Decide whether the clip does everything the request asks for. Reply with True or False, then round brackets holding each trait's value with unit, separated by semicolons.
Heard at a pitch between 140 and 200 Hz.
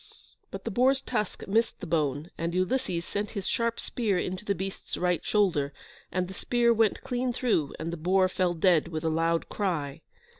True (185 Hz)